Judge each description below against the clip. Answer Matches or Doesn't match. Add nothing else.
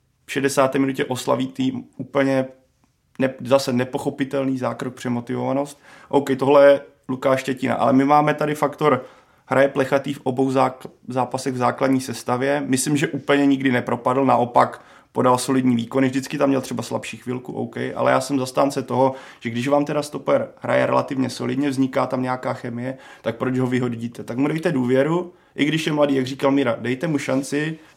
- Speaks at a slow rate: Doesn't match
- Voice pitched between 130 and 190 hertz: Matches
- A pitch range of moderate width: Doesn't match